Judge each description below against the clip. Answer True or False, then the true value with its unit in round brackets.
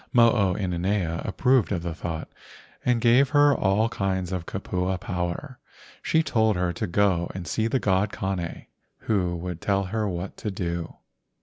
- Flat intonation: False (4.0 semitones)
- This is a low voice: True (95 Hz)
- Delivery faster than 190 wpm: False (175 wpm)